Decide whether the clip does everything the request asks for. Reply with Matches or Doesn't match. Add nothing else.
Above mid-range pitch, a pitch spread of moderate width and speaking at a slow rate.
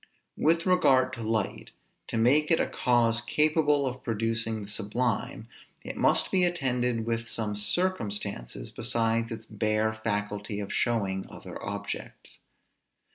Doesn't match